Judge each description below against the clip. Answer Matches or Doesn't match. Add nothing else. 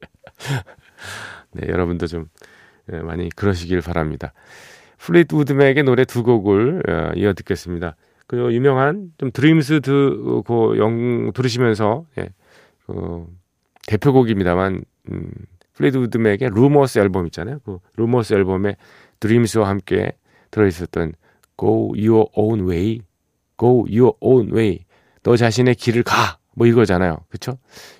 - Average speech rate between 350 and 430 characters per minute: Doesn't match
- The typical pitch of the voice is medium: Doesn't match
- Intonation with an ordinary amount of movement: Doesn't match